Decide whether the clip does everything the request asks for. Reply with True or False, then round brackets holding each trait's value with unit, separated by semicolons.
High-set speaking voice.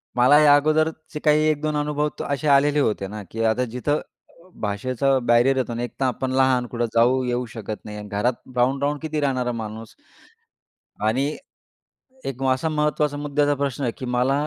False (130 Hz)